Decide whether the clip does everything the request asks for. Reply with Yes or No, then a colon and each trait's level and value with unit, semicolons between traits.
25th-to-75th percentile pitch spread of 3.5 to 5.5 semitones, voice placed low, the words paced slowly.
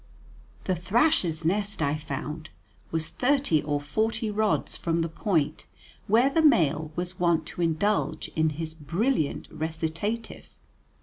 No: average, 5.1 semitones; medium, 170 Hz; slow, 130 wpm